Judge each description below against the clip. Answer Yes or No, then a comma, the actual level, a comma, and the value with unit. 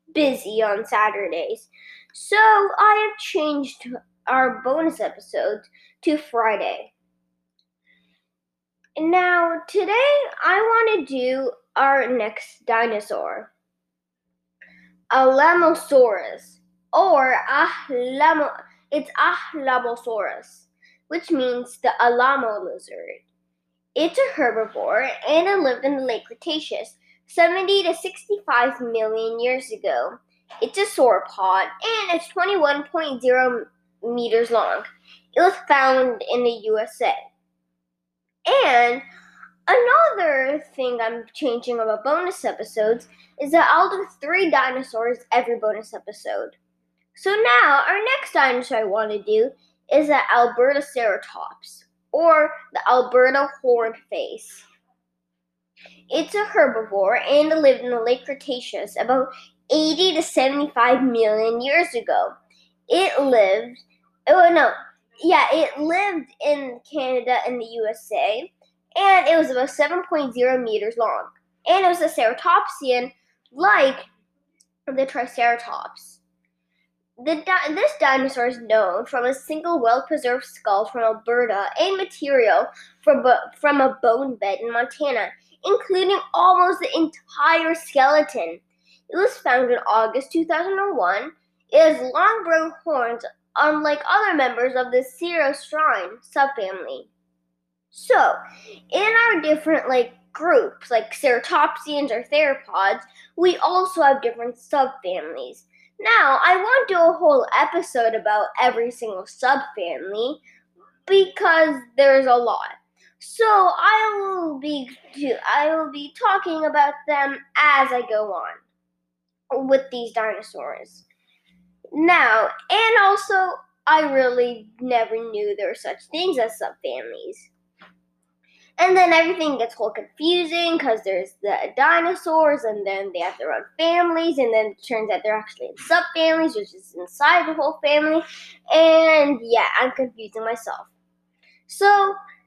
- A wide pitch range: Yes, wide, 6.6 semitones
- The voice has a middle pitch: No, very high, 270 Hz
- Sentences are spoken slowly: Yes, slow, 120 wpm